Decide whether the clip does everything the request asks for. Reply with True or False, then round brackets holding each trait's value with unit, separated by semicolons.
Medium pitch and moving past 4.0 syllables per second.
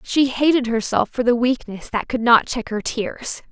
False (240 Hz; 4.5 syllables/s)